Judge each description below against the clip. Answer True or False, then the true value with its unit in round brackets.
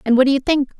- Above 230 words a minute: True (380 wpm)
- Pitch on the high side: True (270 Hz)